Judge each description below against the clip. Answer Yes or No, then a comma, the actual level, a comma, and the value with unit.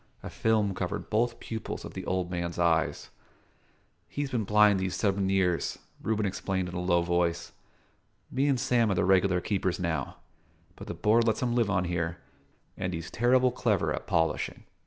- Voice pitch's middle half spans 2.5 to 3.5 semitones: No, average, 4.2 semitones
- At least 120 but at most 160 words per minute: No, average, 180 wpm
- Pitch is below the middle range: Yes, very low, 95 Hz